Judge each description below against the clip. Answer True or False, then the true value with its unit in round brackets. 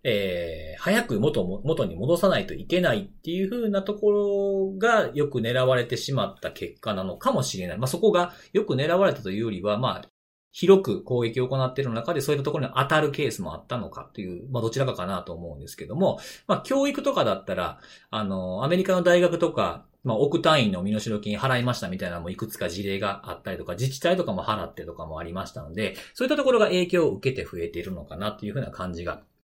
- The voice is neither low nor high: False (130 Hz)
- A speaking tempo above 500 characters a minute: False (455 characters per minute)